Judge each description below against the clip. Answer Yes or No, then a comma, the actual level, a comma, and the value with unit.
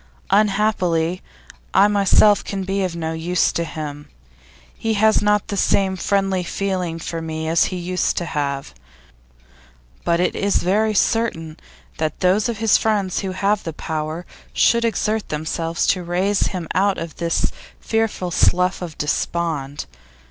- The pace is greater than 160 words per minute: No, average, 150 wpm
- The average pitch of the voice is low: No, medium, 180 Hz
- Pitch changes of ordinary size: Yes, average, 3.6 semitones